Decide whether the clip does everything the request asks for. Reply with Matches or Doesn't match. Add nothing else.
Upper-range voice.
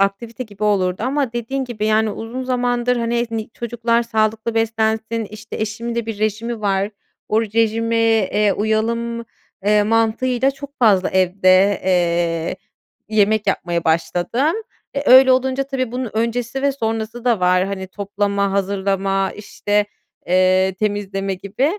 Matches